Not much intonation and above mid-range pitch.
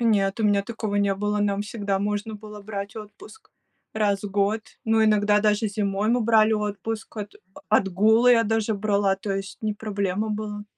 Yes: narrow, 1.5 semitones; high, 210 Hz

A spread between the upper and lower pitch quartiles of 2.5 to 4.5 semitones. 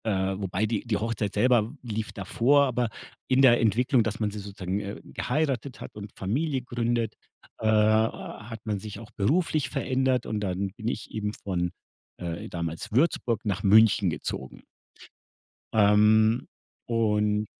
Yes: average, 2.9 semitones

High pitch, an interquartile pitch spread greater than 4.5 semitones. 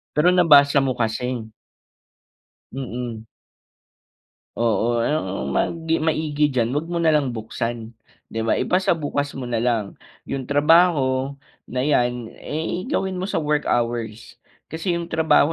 No: low, 135 Hz; average, 5.1 semitones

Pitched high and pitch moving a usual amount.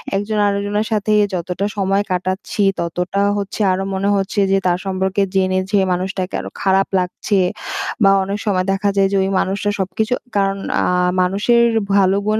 No: high, 195 Hz; narrow, 1.4 semitones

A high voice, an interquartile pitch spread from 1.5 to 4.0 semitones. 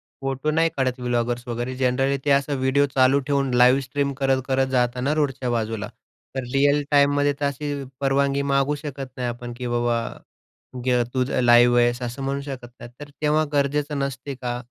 No: low, 135 Hz; narrow, 2.4 semitones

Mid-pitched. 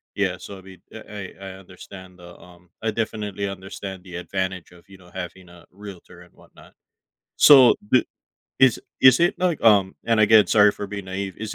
No: very low, 95 Hz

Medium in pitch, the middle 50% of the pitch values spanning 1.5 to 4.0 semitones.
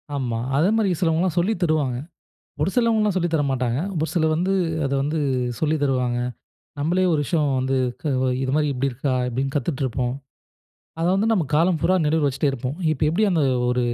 No: medium, 150 Hz; average, 4.6 semitones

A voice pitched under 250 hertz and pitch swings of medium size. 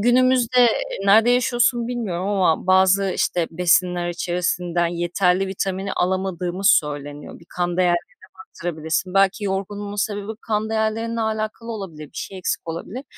Yes: high, 190 Hz; average, 3.7 semitones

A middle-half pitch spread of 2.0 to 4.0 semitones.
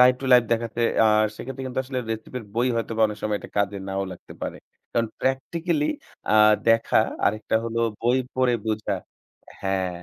Yes: average, 3.0 semitones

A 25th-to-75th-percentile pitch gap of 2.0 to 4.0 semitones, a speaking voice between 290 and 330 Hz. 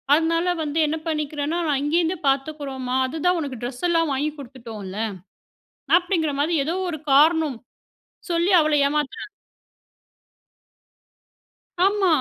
Yes: average, 3.4 semitones; very high, 305 Hz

